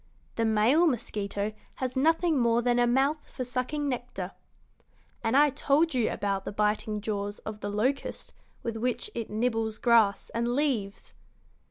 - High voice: Yes, high, 235 Hz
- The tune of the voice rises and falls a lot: No, average, 3.7 semitones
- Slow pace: No, average, 155 wpm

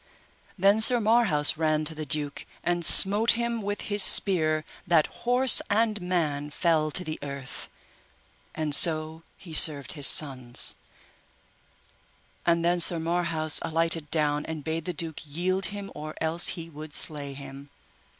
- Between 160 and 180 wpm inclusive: No, average, 150 wpm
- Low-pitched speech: No, medium, 160 Hz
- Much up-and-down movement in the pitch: No, average, 3.3 semitones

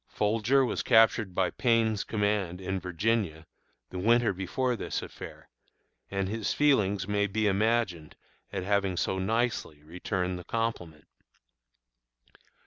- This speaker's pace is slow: Yes, slow, 125 wpm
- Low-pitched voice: Yes, low, 100 Hz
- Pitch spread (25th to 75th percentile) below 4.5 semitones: Yes, average, 3.6 semitones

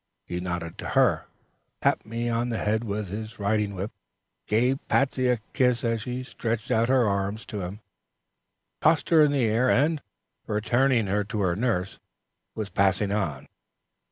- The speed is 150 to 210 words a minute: Yes, average, 165 wpm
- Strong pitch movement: No, average, 3.6 semitones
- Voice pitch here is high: No, low, 110 Hz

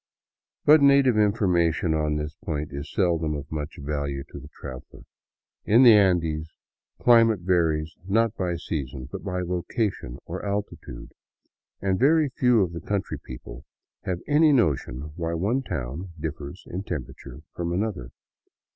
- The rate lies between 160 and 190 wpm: No, average, 145 wpm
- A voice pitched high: No, very low, 85 Hz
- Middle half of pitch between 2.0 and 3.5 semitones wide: No, wide, 5.6 semitones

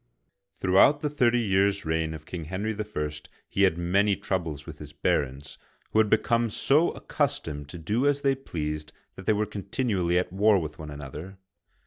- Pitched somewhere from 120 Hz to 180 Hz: No, very low, 95 Hz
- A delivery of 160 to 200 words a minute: Yes, average, 180 wpm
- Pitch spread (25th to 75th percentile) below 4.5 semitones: No, wide, 5.5 semitones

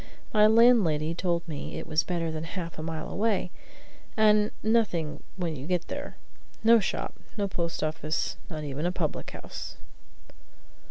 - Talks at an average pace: Yes, average, 155 wpm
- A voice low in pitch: No, medium, 170 Hz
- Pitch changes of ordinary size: Yes, average, 5.0 semitones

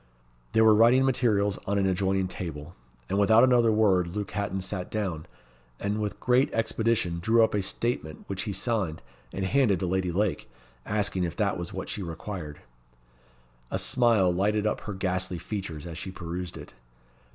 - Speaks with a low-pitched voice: Yes, low, 100 Hz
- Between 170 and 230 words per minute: Yes, average, 175 wpm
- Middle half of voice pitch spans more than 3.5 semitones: No, average, 3.1 semitones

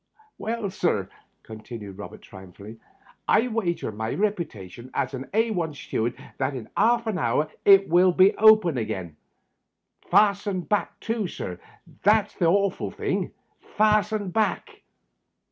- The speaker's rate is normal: No, slow, 130 wpm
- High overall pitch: No, medium, 180 Hz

